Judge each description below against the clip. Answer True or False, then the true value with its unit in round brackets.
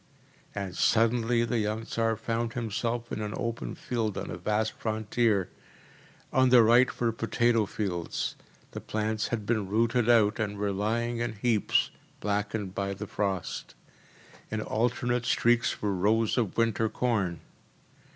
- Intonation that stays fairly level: True (2.2 semitones)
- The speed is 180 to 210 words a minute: False (150 wpm)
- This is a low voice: True (110 Hz)